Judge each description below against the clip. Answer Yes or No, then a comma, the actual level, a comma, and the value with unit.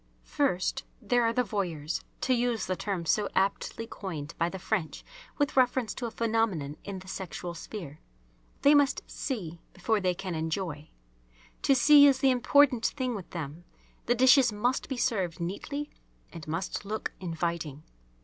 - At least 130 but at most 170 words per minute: Yes, average, 160 wpm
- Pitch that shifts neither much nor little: No, wide, 6.4 semitones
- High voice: Yes, high, 200 Hz